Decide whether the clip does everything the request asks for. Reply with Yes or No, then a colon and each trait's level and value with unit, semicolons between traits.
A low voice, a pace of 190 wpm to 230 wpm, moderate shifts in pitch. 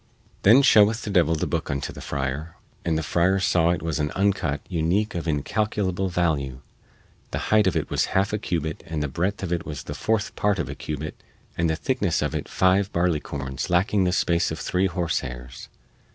Yes: very low, 85 Hz; average, 195 wpm; average, 4.0 semitones